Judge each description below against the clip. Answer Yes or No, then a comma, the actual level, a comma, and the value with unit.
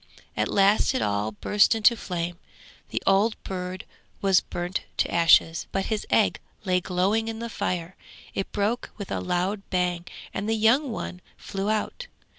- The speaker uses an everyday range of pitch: Yes, average, 3.4 semitones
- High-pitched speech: Yes, high, 195 Hz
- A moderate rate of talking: Yes, average, 165 wpm